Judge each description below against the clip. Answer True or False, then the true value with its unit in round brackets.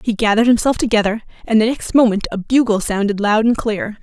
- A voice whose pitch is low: False (220 Hz)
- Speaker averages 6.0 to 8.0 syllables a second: True (6.1 syllables/s)